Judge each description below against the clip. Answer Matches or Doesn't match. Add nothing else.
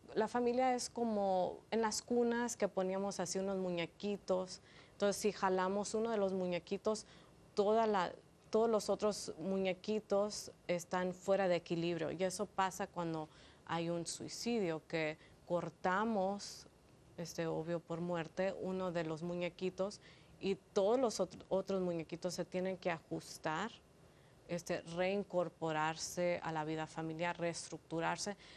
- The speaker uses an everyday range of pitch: Matches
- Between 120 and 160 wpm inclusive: Matches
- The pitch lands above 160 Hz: Matches